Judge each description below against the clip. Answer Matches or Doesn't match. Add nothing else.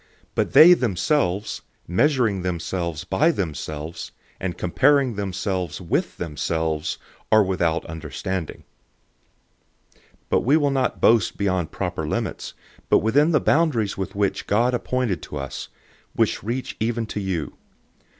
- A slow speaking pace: Matches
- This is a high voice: Doesn't match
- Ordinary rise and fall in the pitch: Doesn't match